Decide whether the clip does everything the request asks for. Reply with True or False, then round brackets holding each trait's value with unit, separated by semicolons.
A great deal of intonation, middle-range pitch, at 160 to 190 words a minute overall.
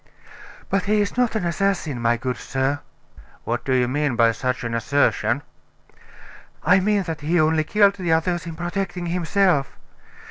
True (6.1 semitones; 160 Hz; 165 wpm)